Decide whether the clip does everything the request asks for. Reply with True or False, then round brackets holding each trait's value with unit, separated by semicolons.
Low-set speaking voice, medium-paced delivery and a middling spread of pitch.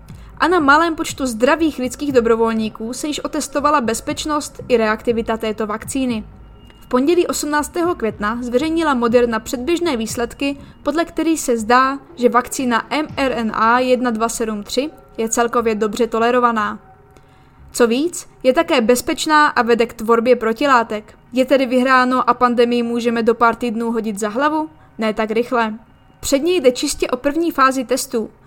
False (250 Hz; 140 wpm; 4.1 semitones)